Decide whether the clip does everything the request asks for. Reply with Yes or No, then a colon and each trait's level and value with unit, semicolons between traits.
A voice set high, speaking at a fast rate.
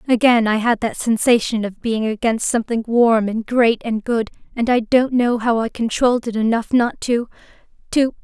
No: high, 230 Hz; average, 180 wpm